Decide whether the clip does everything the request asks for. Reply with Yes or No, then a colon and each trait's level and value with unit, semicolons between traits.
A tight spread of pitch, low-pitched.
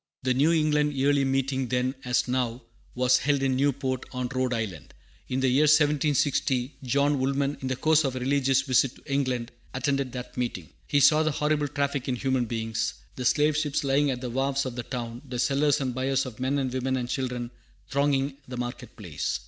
Yes: narrow, 2.1 semitones; low, 130 Hz